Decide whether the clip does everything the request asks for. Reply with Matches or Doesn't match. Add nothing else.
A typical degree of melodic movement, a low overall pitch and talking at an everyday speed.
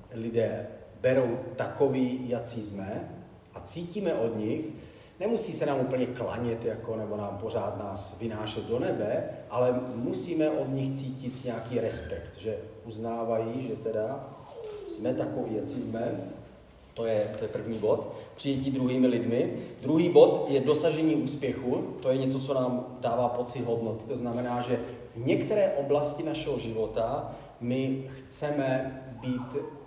Matches